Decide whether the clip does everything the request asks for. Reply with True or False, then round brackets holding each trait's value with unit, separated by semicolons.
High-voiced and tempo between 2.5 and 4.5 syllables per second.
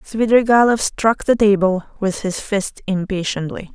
True (205 Hz; 4.4 syllables/s)